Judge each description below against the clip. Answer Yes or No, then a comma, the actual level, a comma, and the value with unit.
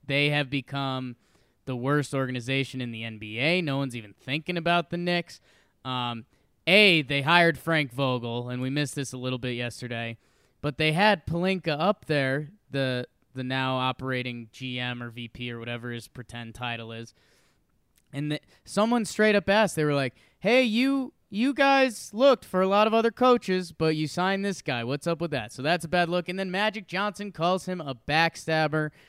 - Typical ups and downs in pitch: No, wide, 6.5 semitones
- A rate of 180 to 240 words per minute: Yes, average, 190 wpm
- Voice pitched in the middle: Yes, medium, 145 Hz